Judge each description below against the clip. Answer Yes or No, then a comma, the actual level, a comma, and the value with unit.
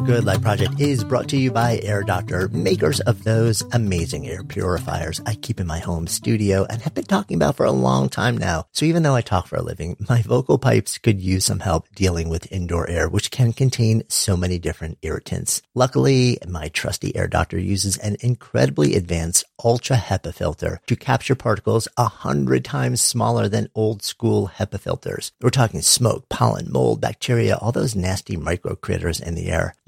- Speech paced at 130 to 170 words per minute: No, average, 190 wpm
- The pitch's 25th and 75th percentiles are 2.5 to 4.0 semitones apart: No, average, 4.9 semitones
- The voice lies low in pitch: Yes, low, 105 Hz